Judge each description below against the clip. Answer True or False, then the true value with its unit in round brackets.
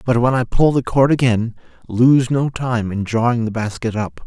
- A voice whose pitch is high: False (120 Hz)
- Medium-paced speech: False (210 wpm)